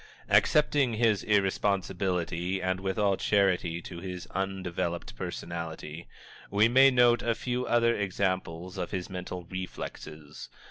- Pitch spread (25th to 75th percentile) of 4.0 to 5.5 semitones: No, average, 3.4 semitones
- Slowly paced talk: Yes, slow, 125 wpm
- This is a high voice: No, very low, 95 Hz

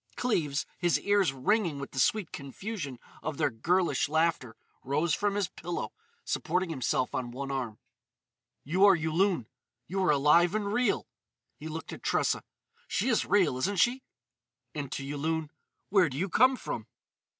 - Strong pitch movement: Yes, wide, 5.9 semitones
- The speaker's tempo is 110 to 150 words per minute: No, average, 160 wpm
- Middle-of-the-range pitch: Yes, medium, 165 Hz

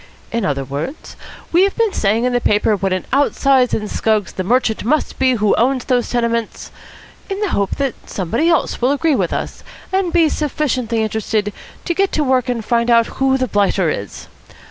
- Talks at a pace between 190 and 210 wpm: Yes, average, 195 wpm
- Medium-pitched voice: No, high, 240 Hz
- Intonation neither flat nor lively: Yes, average, 4.7 semitones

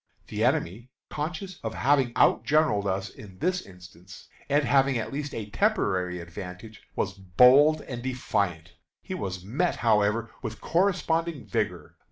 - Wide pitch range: Yes, wide, 7.3 semitones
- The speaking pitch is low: Yes, low, 115 Hz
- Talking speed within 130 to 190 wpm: Yes, average, 140 wpm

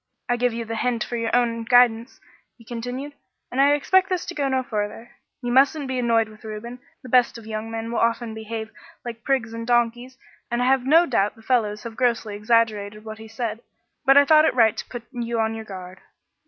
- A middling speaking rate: No, fast, 220 wpm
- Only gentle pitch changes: Yes, narrow, 2.2 semitones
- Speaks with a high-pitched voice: Yes, high, 235 Hz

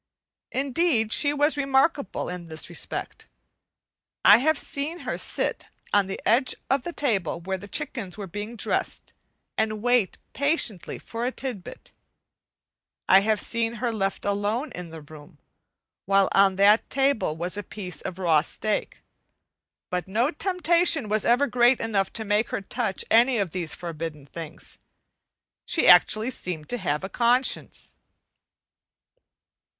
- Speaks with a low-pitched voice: No, high, 215 Hz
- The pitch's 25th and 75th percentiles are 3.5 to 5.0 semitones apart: No, wide, 5.5 semitones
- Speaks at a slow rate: No, average, 145 wpm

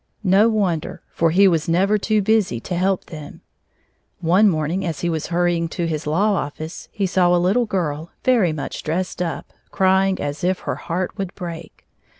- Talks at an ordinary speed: Yes, average, 180 wpm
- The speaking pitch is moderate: Yes, medium, 175 Hz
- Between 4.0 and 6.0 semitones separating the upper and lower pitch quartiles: No, average, 2.9 semitones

